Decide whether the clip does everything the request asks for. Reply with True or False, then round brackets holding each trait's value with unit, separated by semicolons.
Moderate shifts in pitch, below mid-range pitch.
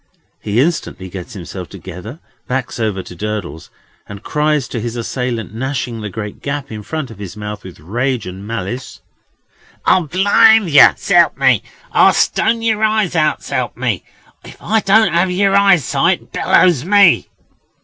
False (9.0 semitones; 130 Hz)